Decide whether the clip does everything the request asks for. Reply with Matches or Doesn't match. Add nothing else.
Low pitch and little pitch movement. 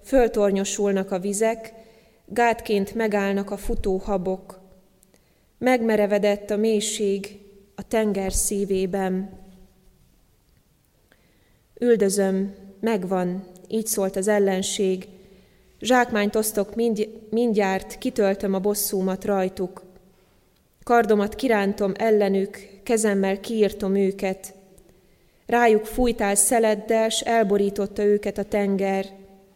Doesn't match